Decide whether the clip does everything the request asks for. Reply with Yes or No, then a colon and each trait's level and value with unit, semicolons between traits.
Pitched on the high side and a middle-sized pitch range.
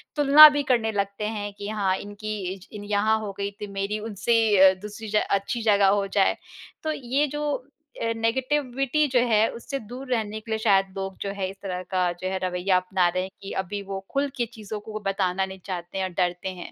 Yes: high, 205 Hz; average, 3.4 semitones